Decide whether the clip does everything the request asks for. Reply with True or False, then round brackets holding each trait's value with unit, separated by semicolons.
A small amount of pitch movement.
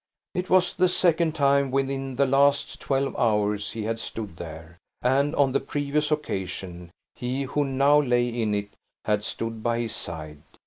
False (5.1 semitones)